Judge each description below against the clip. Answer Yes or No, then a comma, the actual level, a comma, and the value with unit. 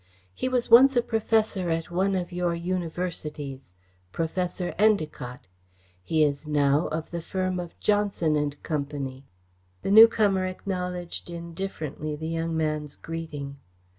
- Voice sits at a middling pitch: Yes, medium, 170 Hz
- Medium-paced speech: No, slow, 130 wpm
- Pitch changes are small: No, average, 3.7 semitones